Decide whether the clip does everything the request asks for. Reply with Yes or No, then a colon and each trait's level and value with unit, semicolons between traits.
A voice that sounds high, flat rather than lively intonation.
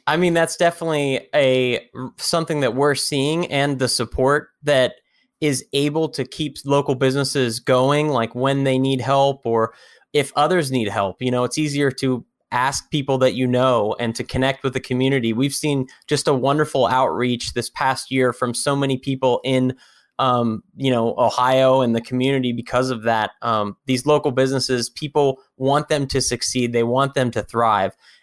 No: low, 130 Hz; narrow, 2.2 semitones